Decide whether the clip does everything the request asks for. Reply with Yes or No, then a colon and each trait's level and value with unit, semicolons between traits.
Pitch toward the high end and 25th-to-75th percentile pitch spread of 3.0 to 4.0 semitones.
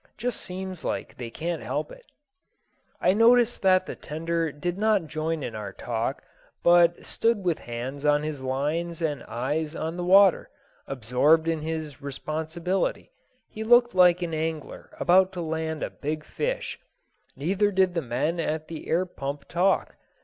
No: medium, 165 Hz; average, 3.7 semitones